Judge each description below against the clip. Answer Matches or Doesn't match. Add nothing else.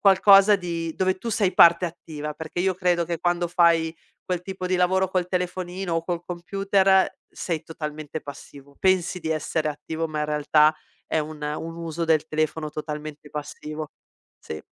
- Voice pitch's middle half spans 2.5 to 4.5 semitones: Matches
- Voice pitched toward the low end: Doesn't match